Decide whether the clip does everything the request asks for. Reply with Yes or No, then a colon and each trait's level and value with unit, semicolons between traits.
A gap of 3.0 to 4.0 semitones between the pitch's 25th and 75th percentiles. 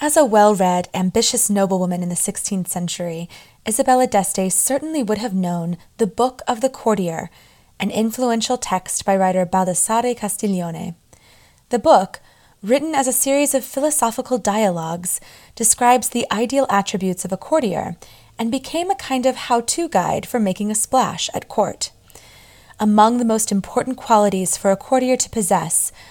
No: average, 5.2 semitones